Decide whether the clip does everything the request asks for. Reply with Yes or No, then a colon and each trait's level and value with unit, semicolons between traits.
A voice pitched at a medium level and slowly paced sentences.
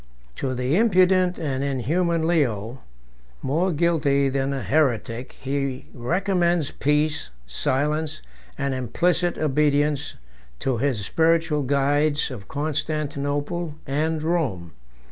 Yes: medium, 145 Hz; slow, 105 wpm